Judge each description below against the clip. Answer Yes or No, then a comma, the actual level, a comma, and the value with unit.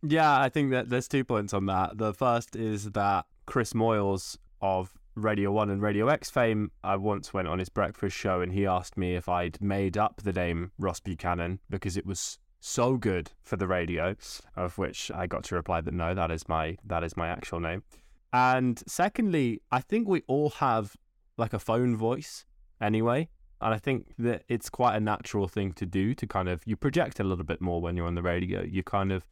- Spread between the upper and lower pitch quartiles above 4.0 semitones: Yes, average, 4.6 semitones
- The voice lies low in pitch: Yes, low, 100 Hz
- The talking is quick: Yes, fast, 215 wpm